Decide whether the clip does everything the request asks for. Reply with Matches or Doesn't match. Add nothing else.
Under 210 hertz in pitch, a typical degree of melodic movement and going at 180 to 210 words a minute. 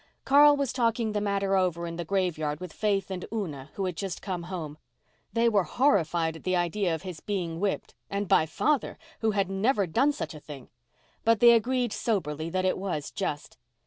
Matches